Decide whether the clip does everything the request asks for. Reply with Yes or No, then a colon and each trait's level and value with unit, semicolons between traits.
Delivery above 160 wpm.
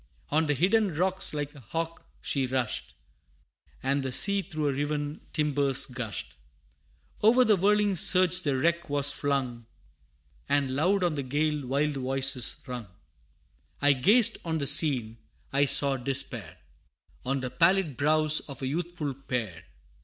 No: average, 145 wpm